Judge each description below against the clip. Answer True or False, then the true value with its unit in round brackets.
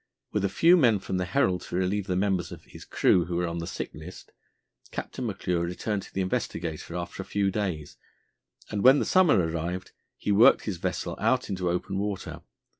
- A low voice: True (95 Hz)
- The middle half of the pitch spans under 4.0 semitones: True (2.7 semitones)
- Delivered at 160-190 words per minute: False (200 wpm)